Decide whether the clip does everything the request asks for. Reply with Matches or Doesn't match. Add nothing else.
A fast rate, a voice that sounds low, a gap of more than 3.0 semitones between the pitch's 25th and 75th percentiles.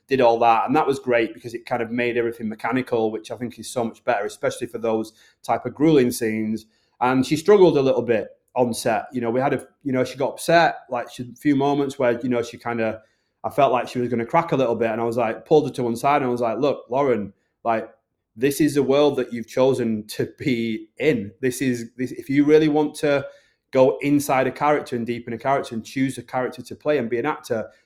Matches